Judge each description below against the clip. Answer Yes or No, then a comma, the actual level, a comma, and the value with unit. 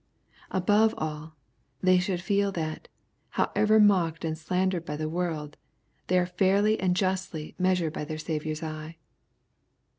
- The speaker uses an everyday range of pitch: Yes, average, 3.2 semitones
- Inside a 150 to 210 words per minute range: No, average, 140 wpm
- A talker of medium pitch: Yes, medium, 180 Hz